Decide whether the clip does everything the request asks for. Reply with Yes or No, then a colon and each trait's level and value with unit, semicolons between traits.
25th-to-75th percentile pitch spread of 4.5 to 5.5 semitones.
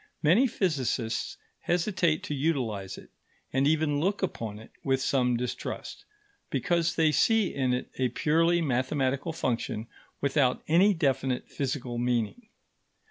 Yes: average, 4.9 semitones